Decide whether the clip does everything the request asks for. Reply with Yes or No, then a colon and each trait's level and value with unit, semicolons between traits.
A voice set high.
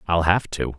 No: very low, 85 Hz